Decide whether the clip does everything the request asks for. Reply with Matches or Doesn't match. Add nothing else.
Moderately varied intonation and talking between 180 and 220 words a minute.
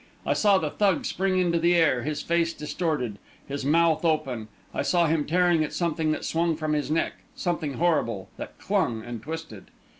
Matches